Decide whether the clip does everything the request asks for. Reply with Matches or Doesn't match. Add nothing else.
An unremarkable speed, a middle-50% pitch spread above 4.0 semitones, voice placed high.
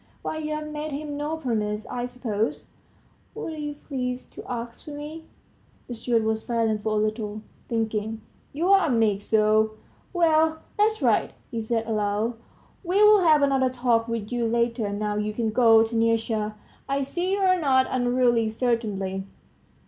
Matches